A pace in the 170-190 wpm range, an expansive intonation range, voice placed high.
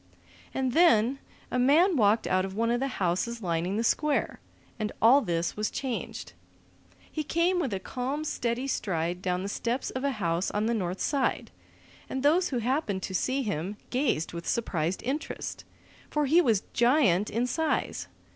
Yes: average, 175 wpm; wide, 6.3 semitones; high, 235 Hz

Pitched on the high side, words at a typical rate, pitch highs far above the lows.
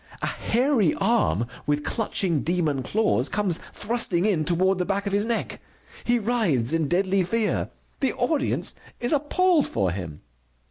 Yes: high, 195 Hz; average, 150 wpm; wide, 6.3 semitones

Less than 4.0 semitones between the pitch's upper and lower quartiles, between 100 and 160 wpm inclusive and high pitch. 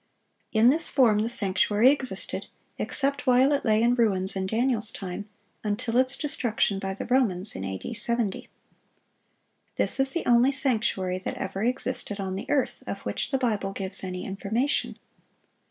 No: average, 4.6 semitones; average, 155 wpm; high, 220 Hz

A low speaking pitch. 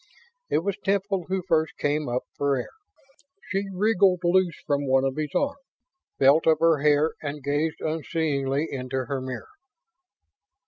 No: medium, 155 Hz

